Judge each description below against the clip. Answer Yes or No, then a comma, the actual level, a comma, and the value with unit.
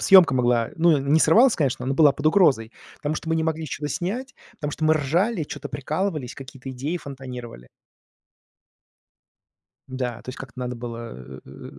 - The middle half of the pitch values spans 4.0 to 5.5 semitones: Yes, average, 4.4 semitones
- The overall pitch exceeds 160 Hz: No, medium, 145 Hz